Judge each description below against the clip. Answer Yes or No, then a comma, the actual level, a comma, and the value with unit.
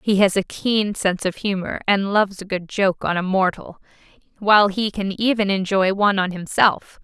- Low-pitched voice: No, high, 195 Hz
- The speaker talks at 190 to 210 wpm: Yes, average, 195 wpm